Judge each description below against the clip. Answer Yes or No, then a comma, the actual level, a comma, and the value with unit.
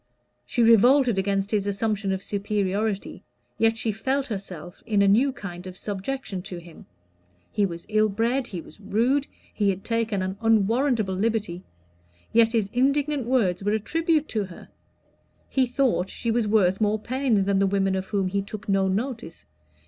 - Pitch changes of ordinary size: Yes, average, 3.3 semitones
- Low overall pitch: No, high, 210 Hz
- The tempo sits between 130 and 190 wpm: Yes, average, 170 wpm